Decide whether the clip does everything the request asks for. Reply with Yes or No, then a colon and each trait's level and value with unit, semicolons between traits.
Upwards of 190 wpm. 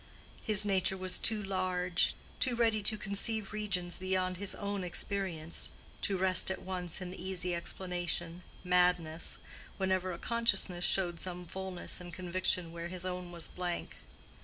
No: average, 150 wpm